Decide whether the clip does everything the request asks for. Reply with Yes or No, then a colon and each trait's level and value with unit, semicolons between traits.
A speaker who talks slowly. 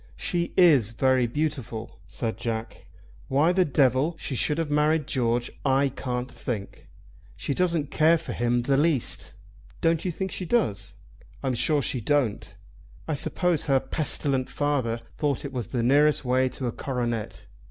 No: average, 160 wpm